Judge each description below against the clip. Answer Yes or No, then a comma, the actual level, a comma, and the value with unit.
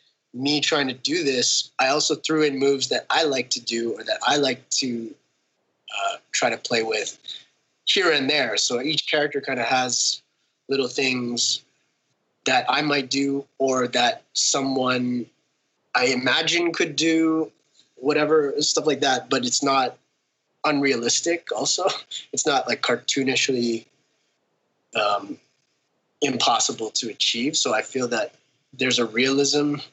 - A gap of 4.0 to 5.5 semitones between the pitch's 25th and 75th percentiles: No, average, 2.8 semitones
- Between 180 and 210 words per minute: No, average, 140 wpm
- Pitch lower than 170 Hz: Yes, medium, 140 Hz